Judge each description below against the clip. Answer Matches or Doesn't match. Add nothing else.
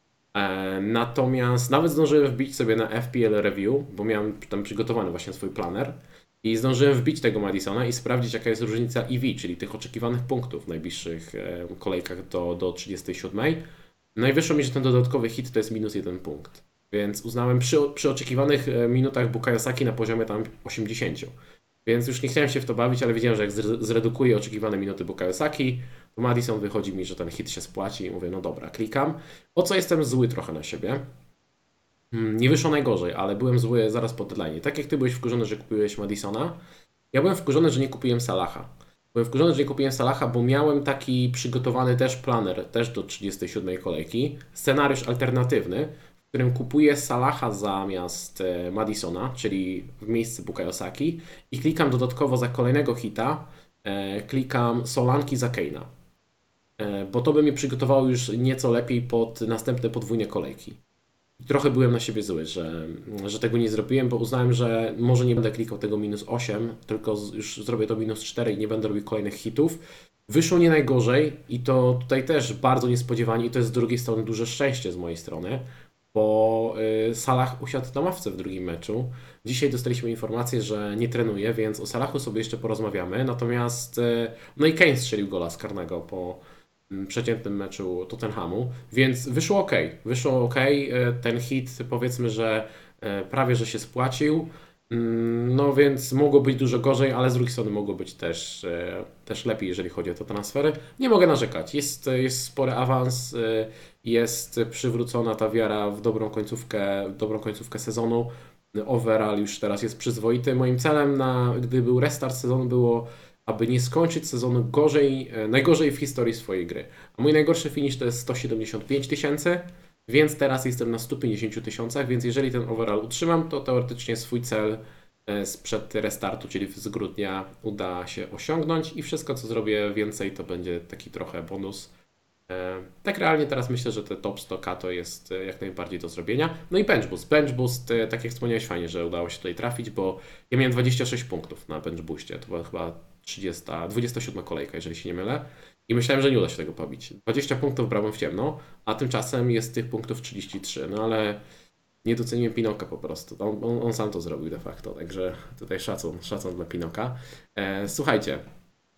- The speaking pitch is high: Doesn't match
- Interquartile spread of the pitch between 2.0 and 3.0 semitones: Doesn't match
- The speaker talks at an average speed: Doesn't match